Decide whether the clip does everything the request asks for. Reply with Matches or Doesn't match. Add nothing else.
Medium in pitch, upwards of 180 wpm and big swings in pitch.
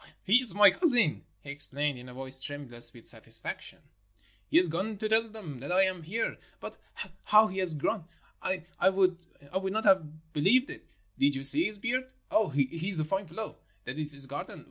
Matches